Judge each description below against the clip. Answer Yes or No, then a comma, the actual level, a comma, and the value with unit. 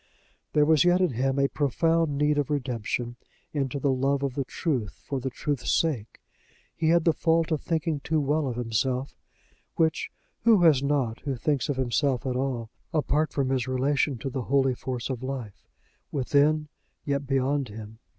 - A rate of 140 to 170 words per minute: No, average, 180 wpm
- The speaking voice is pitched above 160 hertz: No, medium, 140 Hz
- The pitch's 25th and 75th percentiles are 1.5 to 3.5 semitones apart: Yes, average, 2.8 semitones